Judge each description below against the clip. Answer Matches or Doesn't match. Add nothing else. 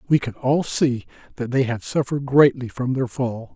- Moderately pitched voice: Doesn't match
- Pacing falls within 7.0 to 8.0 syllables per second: Doesn't match